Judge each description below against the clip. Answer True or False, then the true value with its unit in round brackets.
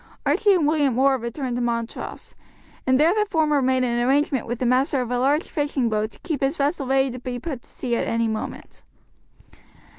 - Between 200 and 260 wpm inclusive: True (205 wpm)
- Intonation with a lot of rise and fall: False (3.4 semitones)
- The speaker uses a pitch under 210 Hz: False (260 Hz)